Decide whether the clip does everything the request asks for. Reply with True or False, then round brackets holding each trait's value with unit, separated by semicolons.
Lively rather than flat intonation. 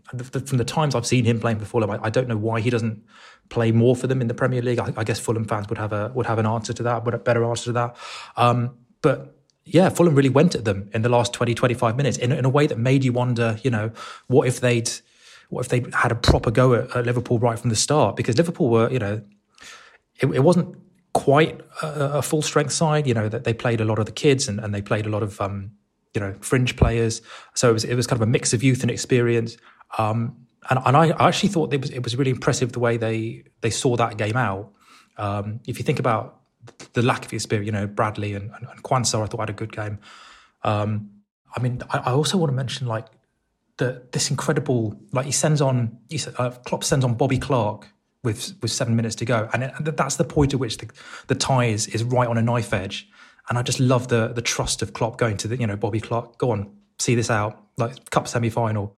False (2.7 semitones)